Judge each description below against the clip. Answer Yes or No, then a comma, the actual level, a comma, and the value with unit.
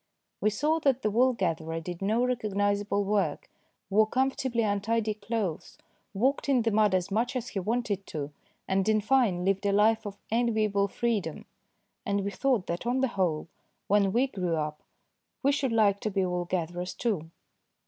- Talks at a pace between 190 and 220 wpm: No, average, 180 wpm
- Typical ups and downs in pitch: Yes, average, 3.6 semitones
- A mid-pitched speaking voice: No, high, 205 Hz